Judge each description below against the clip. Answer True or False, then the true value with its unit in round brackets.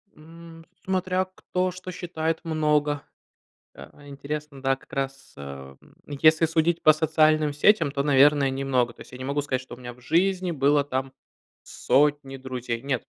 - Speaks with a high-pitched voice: False (145 Hz)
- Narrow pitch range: False (3.2 semitones)